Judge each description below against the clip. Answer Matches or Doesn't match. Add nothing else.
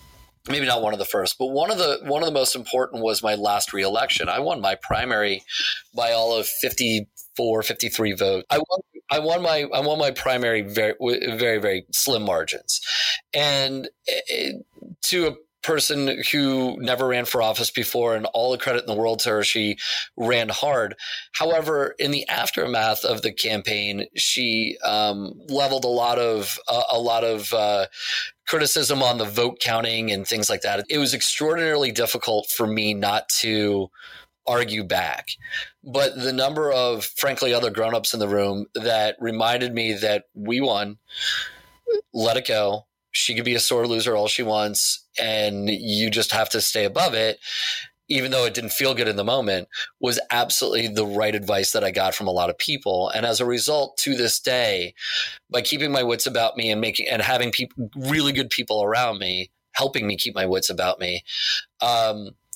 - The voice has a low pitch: Matches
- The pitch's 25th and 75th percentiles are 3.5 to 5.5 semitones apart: Matches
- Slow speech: Doesn't match